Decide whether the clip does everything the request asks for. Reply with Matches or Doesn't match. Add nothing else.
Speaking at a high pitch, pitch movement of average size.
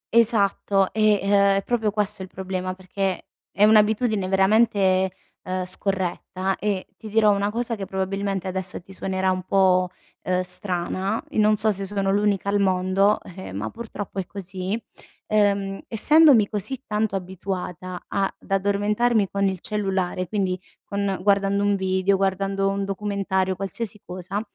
Doesn't match